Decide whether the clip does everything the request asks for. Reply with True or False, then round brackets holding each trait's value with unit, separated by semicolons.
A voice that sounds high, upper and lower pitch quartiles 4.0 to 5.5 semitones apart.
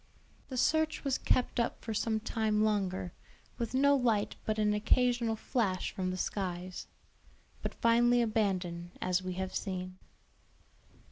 True (215 Hz; 4.4 semitones)